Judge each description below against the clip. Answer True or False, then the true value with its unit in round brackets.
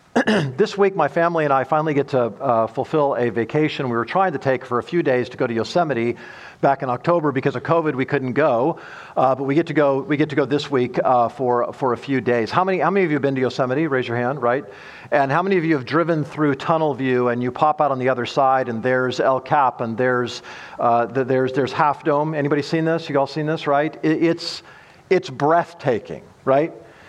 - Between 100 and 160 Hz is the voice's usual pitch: True (140 Hz)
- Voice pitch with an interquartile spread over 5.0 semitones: False (3.9 semitones)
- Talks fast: True (245 wpm)